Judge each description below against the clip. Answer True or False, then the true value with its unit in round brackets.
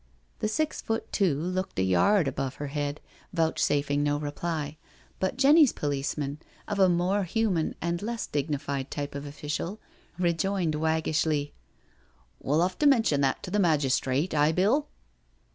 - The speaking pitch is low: False (155 Hz)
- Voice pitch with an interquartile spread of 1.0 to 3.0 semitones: False (4.7 semitones)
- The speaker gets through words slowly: False (155 wpm)